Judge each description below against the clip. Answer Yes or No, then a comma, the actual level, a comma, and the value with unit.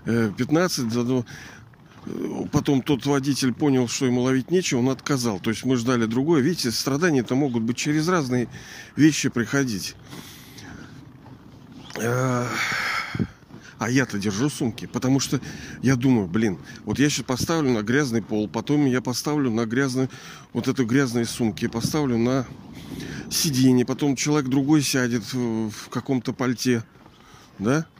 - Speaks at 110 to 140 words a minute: Yes, average, 130 wpm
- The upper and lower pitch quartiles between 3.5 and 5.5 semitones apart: No, average, 3.0 semitones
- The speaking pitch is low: Yes, low, 130 Hz